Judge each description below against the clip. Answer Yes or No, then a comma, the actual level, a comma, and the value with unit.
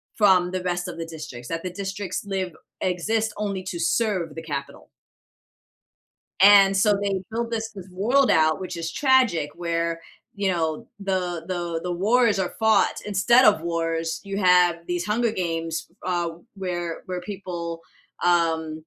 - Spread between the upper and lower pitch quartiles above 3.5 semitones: No, average, 3.2 semitones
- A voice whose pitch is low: No, medium, 180 Hz